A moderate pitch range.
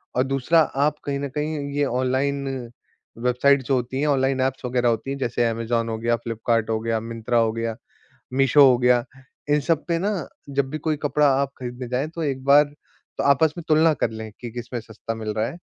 Yes: average, 3.2 semitones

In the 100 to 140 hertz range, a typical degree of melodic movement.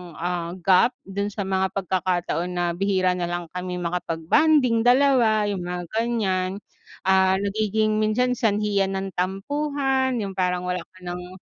No: high, 190 Hz; average, 3.2 semitones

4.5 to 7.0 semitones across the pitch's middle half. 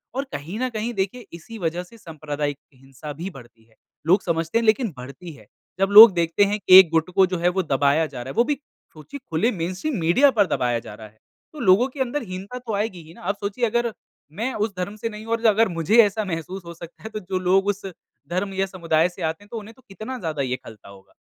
Yes: average, 5.3 semitones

